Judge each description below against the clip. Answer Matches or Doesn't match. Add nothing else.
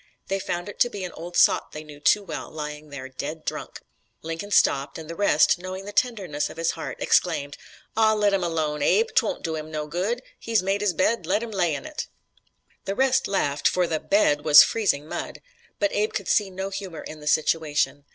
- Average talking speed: Doesn't match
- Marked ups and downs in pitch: Doesn't match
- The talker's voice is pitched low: Doesn't match